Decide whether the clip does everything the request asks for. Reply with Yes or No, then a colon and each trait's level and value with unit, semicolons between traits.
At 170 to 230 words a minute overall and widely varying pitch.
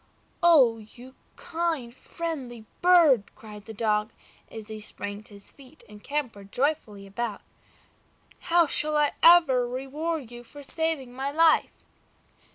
No: slow, 135 wpm; wide, 6.1 semitones